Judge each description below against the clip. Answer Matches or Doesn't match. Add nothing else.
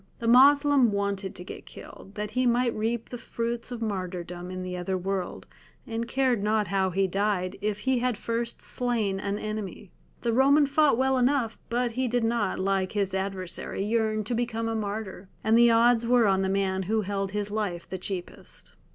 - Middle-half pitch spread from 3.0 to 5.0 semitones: Matches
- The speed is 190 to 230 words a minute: Matches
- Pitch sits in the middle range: Doesn't match